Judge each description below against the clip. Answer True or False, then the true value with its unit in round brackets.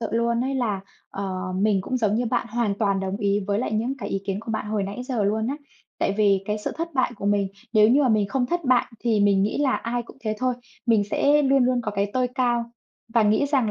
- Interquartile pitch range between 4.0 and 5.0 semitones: False (3.6 semitones)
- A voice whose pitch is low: False (225 Hz)